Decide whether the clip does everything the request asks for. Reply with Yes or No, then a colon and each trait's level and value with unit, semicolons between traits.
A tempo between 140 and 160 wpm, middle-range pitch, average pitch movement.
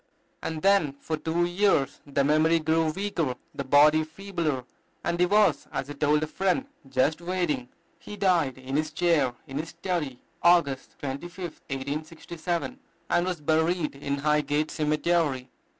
Yes: average, 150 wpm; medium, 155 Hz; average, 3.4 semitones